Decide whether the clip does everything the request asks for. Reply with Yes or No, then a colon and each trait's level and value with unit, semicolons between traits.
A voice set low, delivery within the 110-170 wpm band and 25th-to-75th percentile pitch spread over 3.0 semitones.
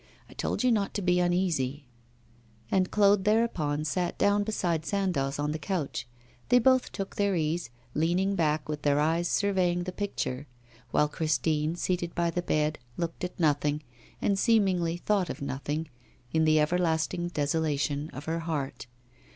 No: medium, 170 Hz; average, 160 wpm; average, 3.8 semitones